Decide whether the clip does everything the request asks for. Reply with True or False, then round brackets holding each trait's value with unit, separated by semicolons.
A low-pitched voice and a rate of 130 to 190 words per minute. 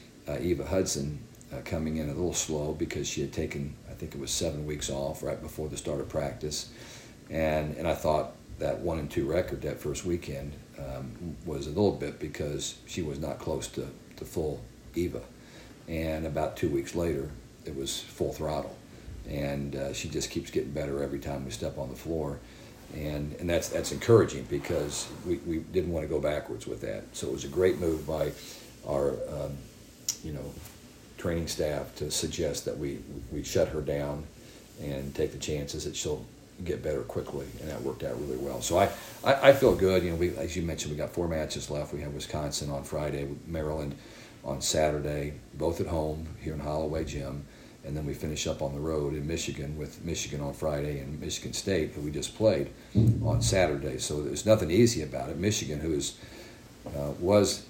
False (75 Hz; 200 wpm)